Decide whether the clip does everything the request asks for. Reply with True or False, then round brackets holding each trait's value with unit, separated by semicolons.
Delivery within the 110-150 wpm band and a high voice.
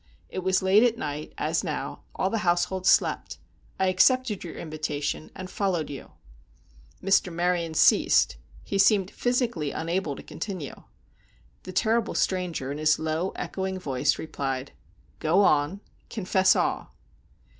False (135 wpm; 180 Hz)